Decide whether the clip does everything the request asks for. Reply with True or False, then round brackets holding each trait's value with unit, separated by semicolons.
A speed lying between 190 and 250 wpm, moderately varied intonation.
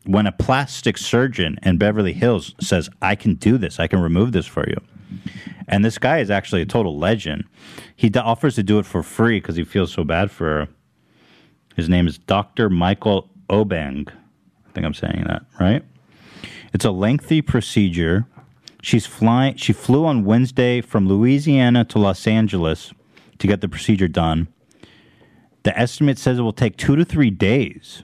False (180 wpm; 4.6 semitones)